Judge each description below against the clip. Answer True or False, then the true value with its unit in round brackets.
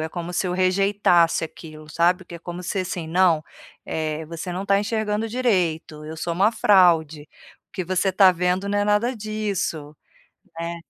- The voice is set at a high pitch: False (180 Hz)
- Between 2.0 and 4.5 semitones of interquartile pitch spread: True (3.4 semitones)